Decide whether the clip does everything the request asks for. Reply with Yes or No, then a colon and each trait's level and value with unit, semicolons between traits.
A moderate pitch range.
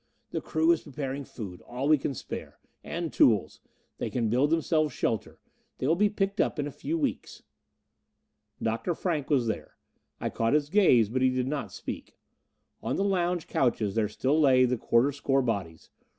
Yes: average, 4.9 semitones